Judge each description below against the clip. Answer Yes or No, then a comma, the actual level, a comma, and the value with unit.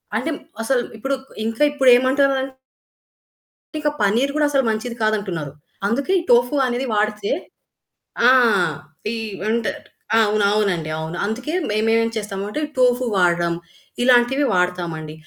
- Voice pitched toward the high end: Yes, high, 225 Hz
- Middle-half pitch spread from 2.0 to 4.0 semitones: No, average, 4.4 semitones